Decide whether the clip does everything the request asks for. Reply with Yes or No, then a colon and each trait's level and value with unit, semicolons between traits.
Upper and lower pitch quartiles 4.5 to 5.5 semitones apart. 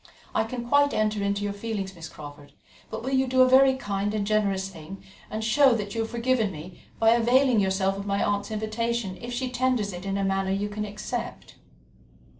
No: average, 3.4 semitones